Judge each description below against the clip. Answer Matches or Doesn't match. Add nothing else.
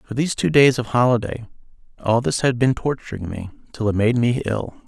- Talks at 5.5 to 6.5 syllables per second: Matches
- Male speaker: Matches